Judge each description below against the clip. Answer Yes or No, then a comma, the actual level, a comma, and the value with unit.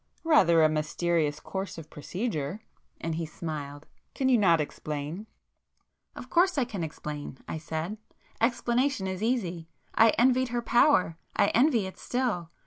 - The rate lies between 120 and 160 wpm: Yes, slow, 135 wpm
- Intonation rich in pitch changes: Yes, wide, 7.1 semitones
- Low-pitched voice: No, medium, 185 Hz